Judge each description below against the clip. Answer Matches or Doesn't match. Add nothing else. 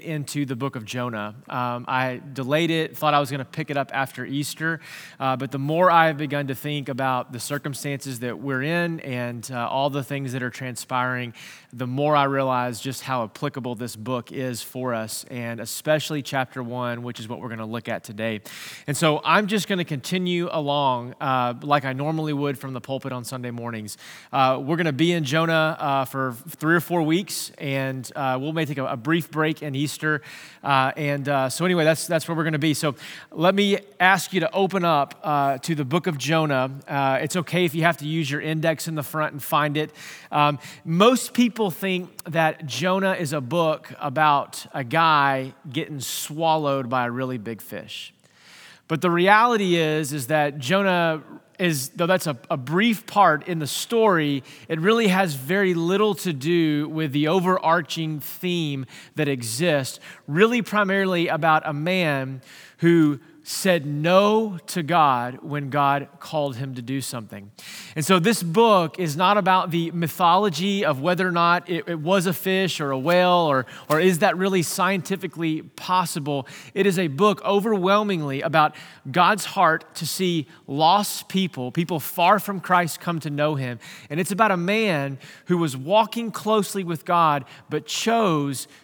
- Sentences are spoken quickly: Doesn't match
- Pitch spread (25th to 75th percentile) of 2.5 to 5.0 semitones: Matches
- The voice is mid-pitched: Matches